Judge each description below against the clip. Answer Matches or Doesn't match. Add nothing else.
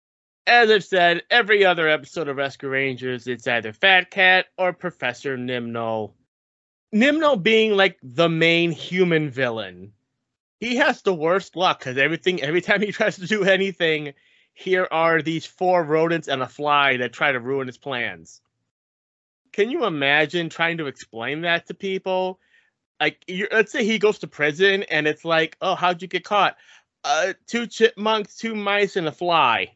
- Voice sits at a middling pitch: Matches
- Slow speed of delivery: Doesn't match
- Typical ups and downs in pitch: Doesn't match